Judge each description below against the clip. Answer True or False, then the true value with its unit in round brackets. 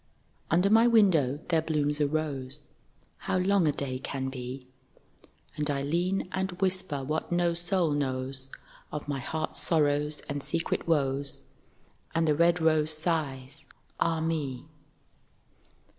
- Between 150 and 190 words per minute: False (135 wpm)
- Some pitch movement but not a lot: True (3.4 semitones)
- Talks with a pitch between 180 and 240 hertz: False (155 Hz)